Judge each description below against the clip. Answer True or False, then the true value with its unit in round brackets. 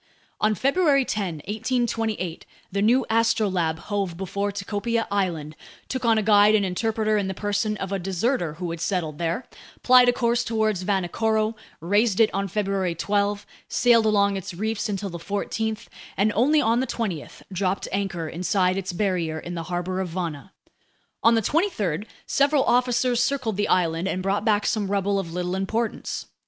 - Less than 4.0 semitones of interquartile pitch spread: True (3.5 semitones)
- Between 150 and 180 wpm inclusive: True (170 wpm)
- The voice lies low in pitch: False (200 Hz)